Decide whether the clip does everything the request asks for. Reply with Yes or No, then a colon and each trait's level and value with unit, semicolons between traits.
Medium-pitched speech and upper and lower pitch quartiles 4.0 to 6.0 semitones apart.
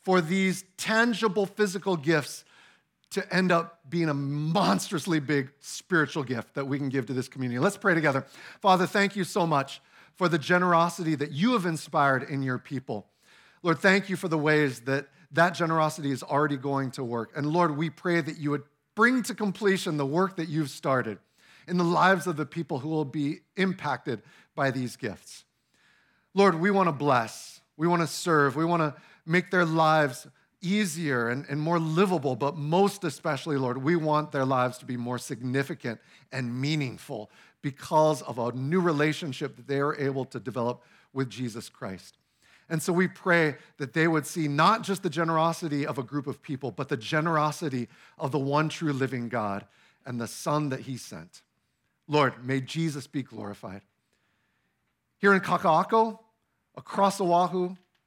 Yes: medium, 155 Hz; average, 4.3 semitones